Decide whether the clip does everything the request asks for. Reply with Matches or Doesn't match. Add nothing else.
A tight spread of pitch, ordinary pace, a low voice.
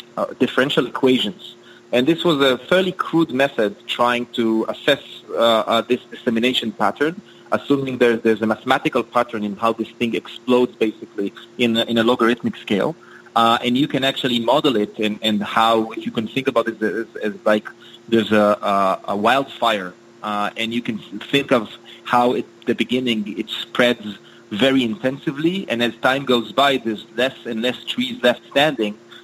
Matches